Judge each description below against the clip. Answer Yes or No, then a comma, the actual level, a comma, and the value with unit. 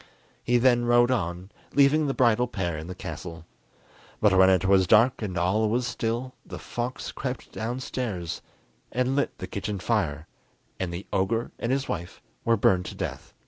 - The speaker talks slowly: No, average, 175 wpm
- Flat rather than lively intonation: No, average, 5.0 semitones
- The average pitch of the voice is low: Yes, low, 110 Hz